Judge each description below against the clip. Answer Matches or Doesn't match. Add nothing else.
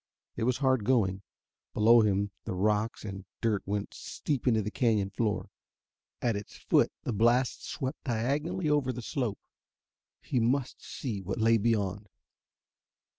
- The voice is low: Matches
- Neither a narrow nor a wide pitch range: Matches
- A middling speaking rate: Matches